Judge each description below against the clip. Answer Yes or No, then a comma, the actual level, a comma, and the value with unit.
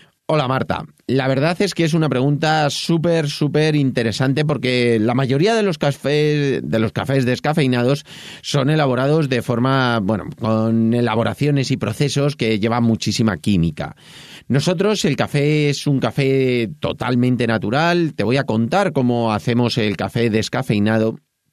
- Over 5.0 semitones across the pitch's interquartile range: No, average, 4.1 semitones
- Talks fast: No, average, 145 wpm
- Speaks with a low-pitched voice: Yes, low, 130 Hz